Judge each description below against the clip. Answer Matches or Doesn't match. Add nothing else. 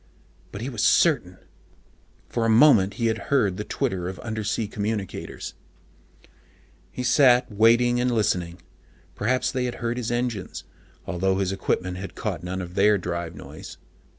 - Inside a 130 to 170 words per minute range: Matches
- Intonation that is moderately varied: Matches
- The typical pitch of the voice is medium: Doesn't match